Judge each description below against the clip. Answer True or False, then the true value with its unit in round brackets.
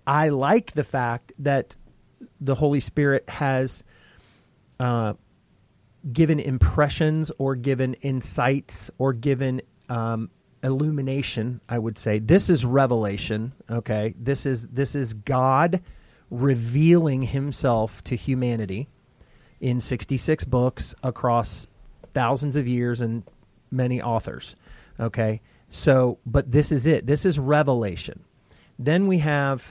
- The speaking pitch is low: True (130 Hz)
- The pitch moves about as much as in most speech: True (3.3 semitones)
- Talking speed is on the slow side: True (115 wpm)